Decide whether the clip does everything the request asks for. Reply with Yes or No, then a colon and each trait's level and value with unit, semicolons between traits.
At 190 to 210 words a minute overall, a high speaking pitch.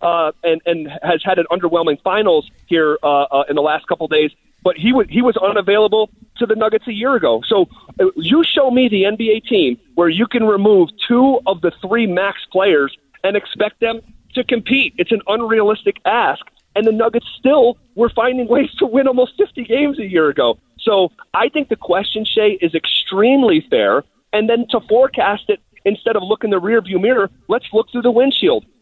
Yes: average, 200 wpm; high, 215 Hz